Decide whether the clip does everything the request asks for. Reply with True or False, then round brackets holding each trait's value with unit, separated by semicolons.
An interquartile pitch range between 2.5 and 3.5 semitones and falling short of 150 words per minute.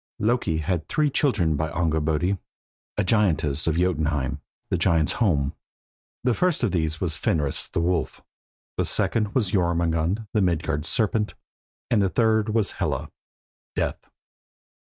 False (5.2 semitones; 135 wpm)